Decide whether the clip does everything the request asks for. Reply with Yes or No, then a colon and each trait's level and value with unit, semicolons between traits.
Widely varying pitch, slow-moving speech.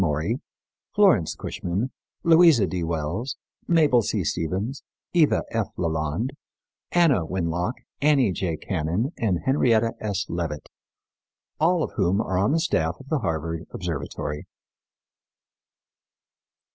Yes: wide, 8.4 semitones; slow, 115 wpm